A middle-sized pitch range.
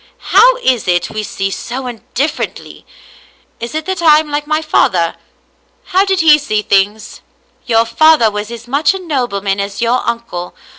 No: wide, 6.8 semitones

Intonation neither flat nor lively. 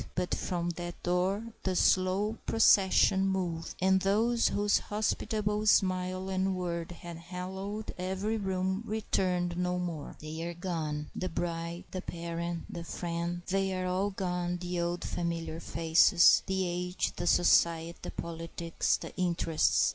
No: narrow, 1.9 semitones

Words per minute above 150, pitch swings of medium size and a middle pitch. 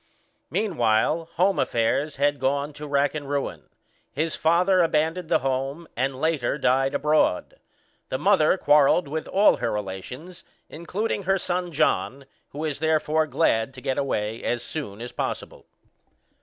No: average, 145 wpm; average, 3.7 semitones; medium, 150 Hz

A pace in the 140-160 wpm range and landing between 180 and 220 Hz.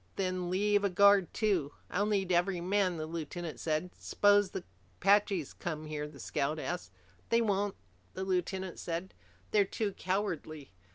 Yes: average, 155 wpm; medium, 185 Hz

